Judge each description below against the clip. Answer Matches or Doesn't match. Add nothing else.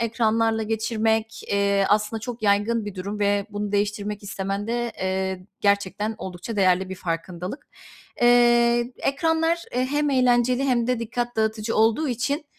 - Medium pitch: Doesn't match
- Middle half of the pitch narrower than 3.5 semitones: Matches